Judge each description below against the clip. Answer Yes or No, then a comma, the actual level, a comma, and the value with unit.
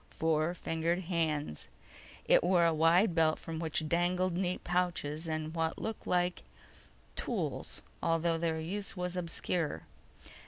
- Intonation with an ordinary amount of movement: No, narrow, 1.9 semitones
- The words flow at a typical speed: No, slow, 130 wpm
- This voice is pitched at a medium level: Yes, medium, 170 Hz